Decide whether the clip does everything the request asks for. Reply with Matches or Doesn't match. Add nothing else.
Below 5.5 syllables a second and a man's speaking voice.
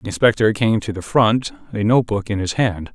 Doesn't match